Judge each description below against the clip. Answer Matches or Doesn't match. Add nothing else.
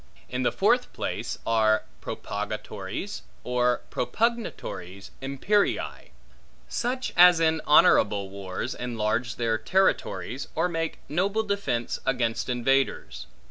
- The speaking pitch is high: Doesn't match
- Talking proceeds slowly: Matches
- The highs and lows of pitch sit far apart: Matches